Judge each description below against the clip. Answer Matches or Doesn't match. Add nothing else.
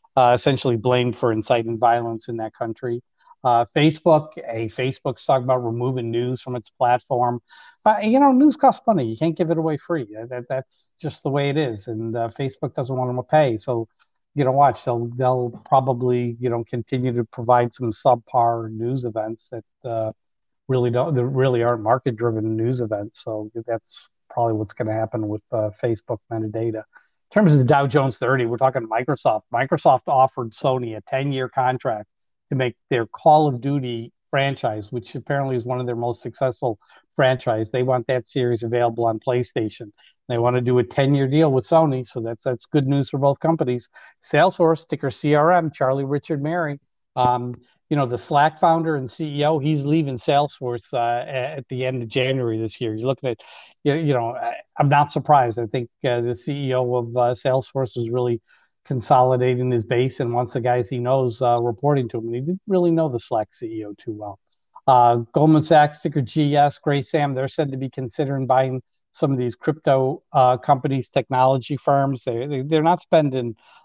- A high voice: Doesn't match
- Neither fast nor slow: Matches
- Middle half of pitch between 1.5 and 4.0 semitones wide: Matches